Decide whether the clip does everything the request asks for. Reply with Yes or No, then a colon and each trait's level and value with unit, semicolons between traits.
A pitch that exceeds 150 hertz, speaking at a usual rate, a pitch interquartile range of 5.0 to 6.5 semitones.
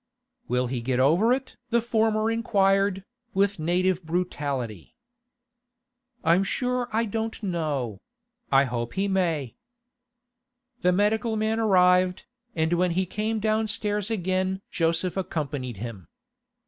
No: medium, 185 Hz; slow, 120 wpm; wide, 5.6 semitones